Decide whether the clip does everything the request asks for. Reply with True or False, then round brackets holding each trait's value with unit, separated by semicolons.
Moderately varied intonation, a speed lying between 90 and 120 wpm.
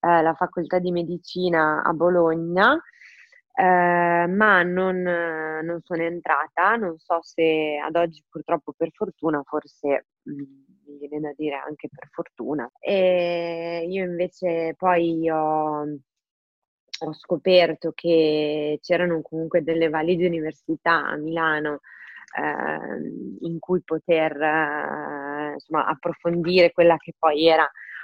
False (2.2 semitones; 115 wpm)